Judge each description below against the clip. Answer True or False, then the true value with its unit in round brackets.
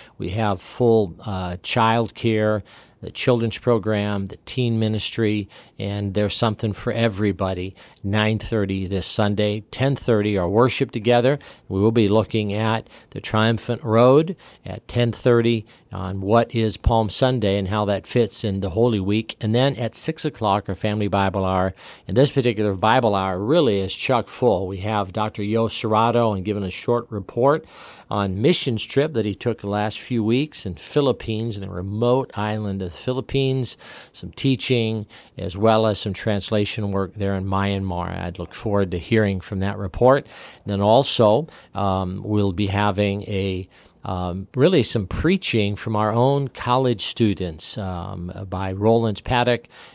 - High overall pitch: False (105 Hz)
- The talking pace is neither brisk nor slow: True (160 wpm)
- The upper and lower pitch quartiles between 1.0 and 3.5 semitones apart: True (3.1 semitones)